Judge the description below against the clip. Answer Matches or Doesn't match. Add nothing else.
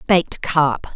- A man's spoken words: Doesn't match